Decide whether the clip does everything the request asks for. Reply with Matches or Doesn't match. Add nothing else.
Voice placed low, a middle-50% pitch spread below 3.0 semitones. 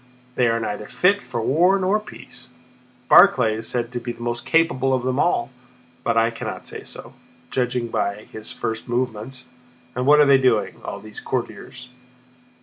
Matches